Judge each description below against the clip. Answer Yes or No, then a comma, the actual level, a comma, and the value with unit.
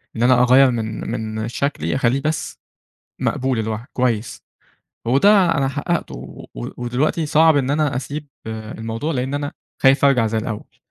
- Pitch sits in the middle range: No, low, 125 Hz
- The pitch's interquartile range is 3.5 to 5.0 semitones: Yes, average, 4.0 semitones